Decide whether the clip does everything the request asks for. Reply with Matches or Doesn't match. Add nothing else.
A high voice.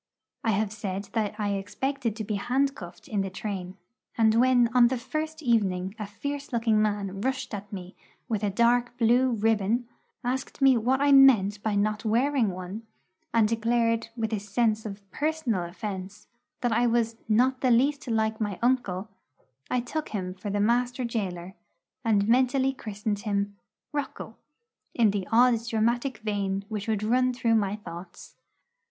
Matches